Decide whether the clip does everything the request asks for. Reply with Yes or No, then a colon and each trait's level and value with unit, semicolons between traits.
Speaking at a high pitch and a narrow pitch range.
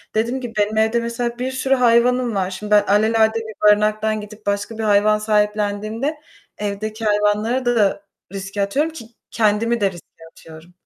Yes: high, 215 Hz; narrow, 2.1 semitones